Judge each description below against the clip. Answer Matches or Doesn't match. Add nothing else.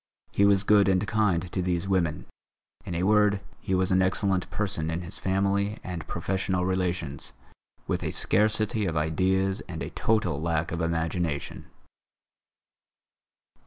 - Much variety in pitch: Doesn't match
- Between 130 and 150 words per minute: Matches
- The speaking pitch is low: Matches